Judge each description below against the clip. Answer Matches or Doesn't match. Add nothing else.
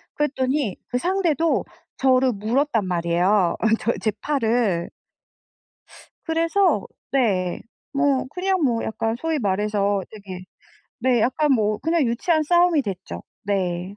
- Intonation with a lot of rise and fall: Matches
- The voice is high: Matches